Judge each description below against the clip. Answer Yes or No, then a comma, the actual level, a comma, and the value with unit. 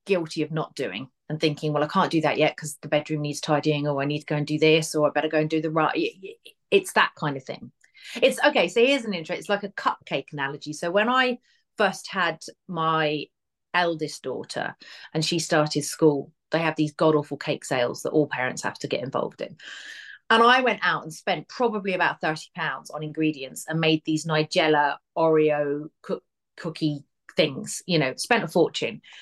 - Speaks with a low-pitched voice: No, medium, 155 Hz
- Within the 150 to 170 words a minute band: No, fast, 205 wpm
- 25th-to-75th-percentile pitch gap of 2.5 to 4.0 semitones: Yes, average, 2.9 semitones